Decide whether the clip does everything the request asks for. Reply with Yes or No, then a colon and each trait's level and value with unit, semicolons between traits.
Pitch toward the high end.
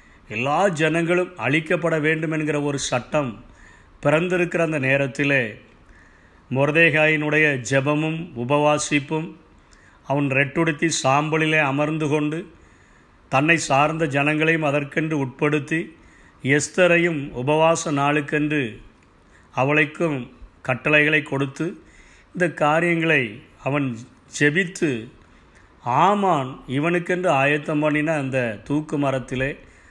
No: medium, 145 Hz